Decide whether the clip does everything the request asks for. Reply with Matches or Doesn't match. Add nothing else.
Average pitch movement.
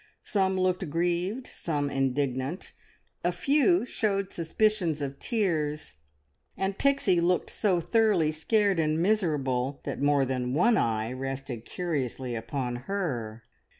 Doesn't match